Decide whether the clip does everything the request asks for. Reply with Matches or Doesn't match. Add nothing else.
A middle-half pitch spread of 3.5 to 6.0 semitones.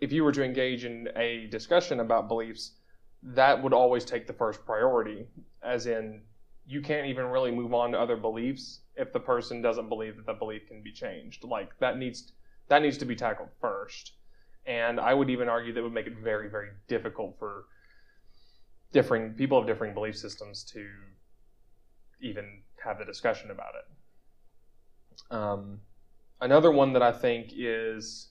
Doesn't match